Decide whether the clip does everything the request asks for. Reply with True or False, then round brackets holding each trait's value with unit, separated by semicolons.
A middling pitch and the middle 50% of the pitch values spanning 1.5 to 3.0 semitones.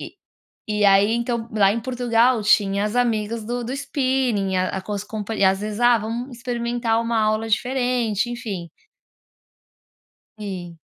False (225 Hz; 2.7 semitones)